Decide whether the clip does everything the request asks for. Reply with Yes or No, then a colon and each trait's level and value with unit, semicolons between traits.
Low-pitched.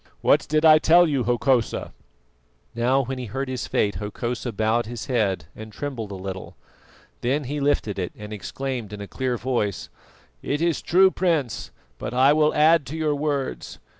Yes: low, 130 Hz